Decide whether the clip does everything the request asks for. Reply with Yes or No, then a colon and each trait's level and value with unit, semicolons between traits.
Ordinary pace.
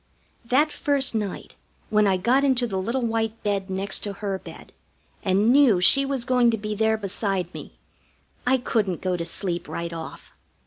Yes: average, 180 wpm